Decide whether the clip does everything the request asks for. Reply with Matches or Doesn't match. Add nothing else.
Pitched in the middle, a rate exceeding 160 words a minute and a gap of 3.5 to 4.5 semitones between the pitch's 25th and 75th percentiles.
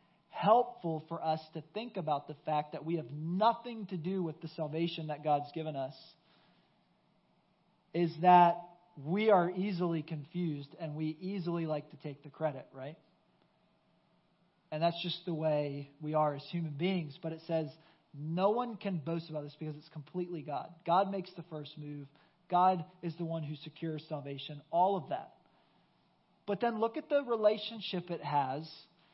Doesn't match